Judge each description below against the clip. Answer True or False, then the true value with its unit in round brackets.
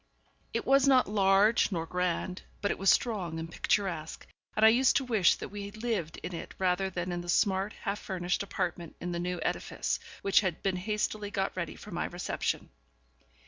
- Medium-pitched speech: False (195 Hz)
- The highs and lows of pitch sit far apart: False (3.1 semitones)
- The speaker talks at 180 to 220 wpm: True (190 wpm)